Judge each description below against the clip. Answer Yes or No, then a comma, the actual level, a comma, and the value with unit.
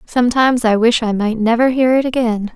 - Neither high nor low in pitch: No, high, 235 Hz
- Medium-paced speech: No, fast, 210 wpm